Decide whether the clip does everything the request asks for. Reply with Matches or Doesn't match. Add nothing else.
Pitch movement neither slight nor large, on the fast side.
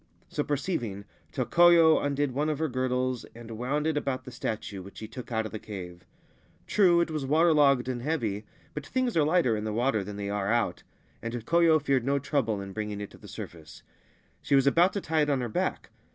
Doesn't match